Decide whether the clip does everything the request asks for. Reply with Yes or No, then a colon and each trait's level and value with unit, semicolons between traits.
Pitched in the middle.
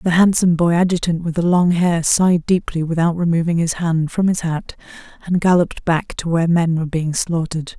Yes: medium, 170 Hz